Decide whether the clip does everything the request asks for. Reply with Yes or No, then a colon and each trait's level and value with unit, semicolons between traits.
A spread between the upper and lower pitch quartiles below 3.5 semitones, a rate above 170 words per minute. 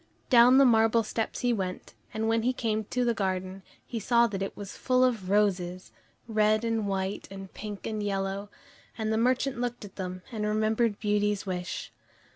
Yes: average, 3.0 semitones; average, 185 wpm